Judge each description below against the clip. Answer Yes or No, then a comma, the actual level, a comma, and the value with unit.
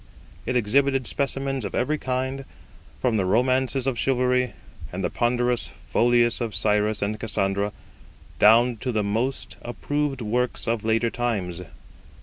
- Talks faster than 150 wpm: No, slow, 135 wpm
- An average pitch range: Yes, average, 3.2 semitones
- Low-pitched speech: Yes, low, 120 Hz